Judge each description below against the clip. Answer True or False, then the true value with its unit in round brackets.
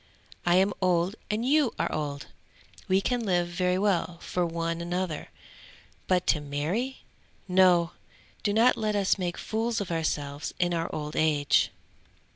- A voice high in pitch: False (180 Hz)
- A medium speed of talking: True (150 wpm)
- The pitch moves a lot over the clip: False (3.5 semitones)